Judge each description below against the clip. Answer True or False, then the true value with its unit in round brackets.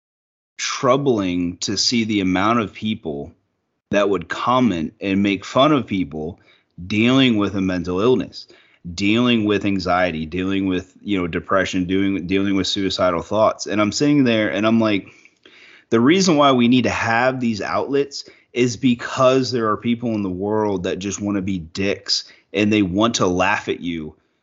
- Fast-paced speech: False (170 wpm)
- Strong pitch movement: False (3.7 semitones)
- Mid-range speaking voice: False (100 Hz)